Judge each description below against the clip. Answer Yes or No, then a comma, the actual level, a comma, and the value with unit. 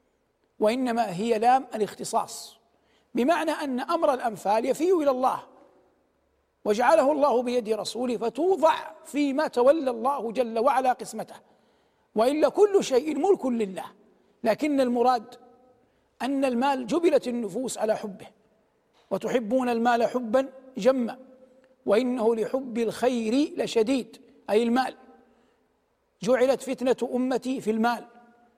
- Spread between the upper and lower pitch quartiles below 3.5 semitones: Yes, narrow, 2.5 semitones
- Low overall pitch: No, very high, 250 Hz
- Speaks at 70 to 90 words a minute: No, average, 105 wpm